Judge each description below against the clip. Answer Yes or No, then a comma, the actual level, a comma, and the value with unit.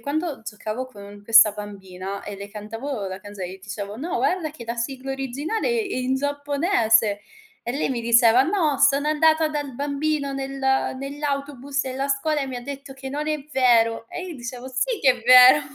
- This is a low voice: No, very high, 265 Hz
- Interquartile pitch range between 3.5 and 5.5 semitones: Yes, average, 4.1 semitones